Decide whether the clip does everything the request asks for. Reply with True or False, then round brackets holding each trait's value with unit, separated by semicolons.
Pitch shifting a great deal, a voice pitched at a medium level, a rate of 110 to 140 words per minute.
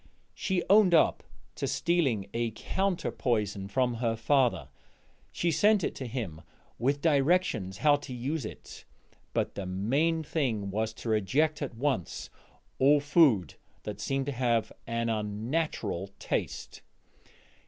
False (6.0 semitones; 125 Hz; 135 wpm)